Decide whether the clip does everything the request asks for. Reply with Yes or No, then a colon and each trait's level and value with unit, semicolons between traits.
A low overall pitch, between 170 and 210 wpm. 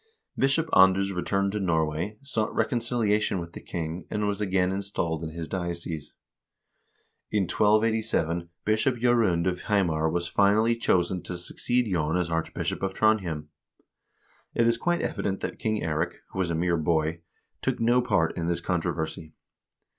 No: very low, 95 Hz; average, 155 wpm